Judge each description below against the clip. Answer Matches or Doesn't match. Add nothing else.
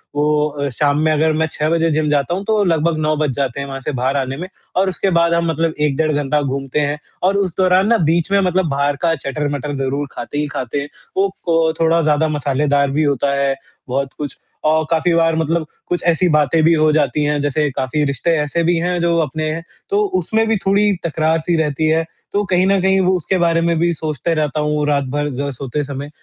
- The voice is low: Doesn't match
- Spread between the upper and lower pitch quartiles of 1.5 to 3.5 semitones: Matches